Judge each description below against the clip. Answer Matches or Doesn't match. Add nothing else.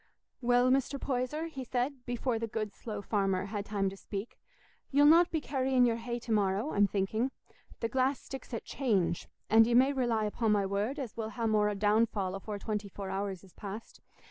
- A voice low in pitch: Doesn't match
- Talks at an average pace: Matches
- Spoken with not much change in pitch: Doesn't match